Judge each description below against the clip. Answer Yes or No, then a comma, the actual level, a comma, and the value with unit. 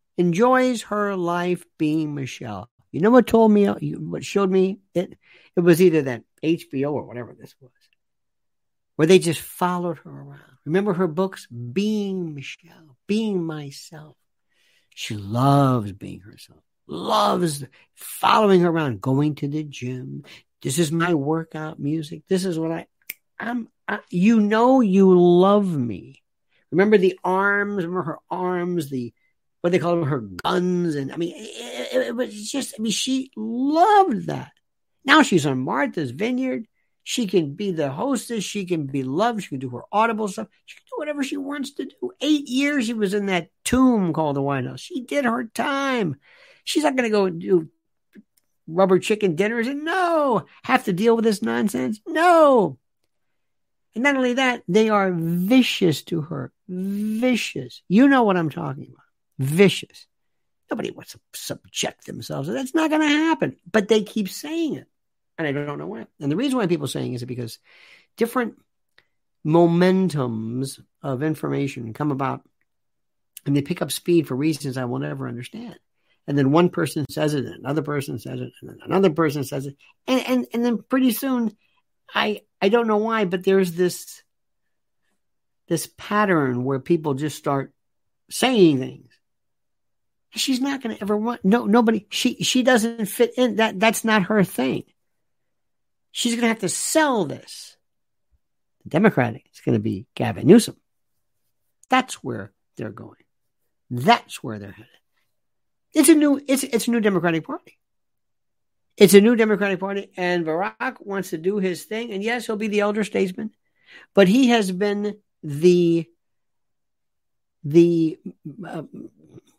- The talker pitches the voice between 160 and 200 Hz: Yes, medium, 185 Hz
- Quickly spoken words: No, average, 165 wpm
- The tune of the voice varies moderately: No, wide, 7.6 semitones